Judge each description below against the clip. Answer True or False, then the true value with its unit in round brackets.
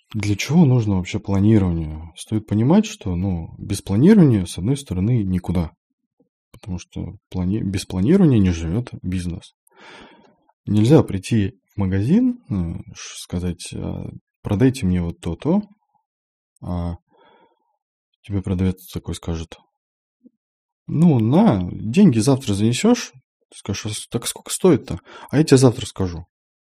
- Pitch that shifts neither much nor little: False (8.5 semitones)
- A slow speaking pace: False (120 wpm)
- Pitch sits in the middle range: False (105 Hz)